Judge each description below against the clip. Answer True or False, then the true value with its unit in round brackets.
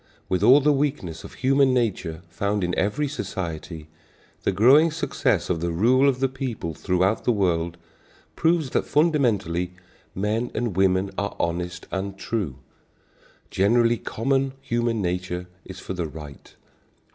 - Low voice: True (100 Hz)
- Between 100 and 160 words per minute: True (145 wpm)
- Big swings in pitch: True (6.6 semitones)